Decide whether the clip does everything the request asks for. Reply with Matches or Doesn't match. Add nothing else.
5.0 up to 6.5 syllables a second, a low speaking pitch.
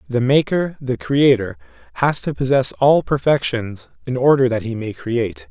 Doesn't match